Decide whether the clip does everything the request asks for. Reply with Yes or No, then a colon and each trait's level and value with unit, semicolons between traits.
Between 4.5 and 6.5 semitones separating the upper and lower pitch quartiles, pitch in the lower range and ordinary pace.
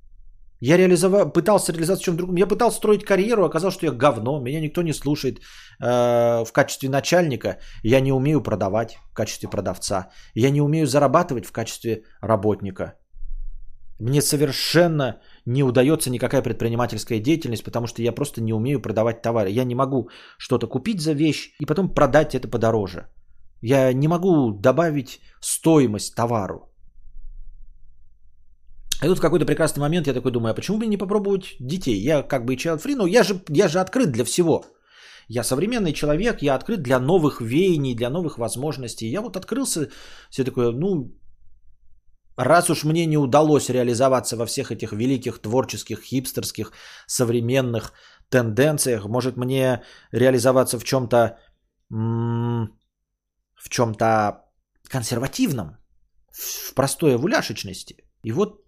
Yes: average, 5.3 semitones; low, 130 Hz; average, 145 wpm